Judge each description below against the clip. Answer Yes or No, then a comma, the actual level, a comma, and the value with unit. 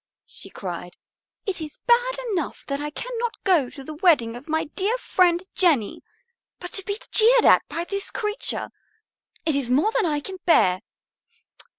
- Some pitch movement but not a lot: No, wide, 6.6 semitones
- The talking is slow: No, average, 170 wpm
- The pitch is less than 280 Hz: No, very high, 345 Hz